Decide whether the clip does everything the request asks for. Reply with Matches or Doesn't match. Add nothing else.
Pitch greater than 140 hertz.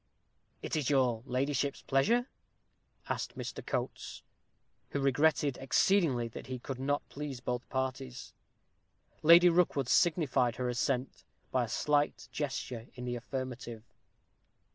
Doesn't match